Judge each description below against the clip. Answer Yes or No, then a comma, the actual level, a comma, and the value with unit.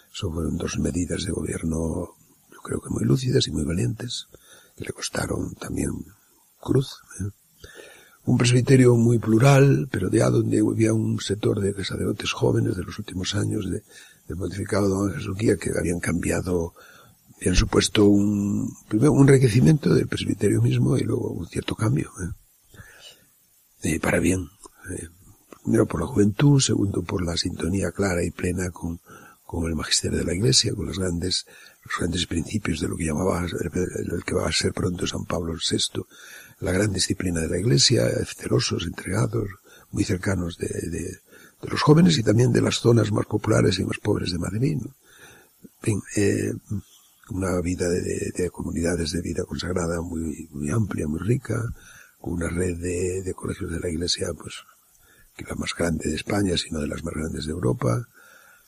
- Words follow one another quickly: No, average, 175 wpm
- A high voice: No, very low, 95 Hz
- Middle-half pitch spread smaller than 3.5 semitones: No, average, 4.0 semitones